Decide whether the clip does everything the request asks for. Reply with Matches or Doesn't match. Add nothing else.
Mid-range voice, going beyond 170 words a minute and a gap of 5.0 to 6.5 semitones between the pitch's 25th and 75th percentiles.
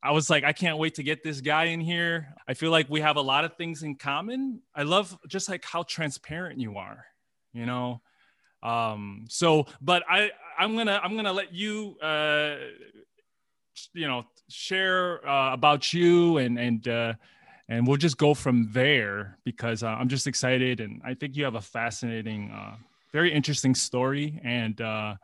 Matches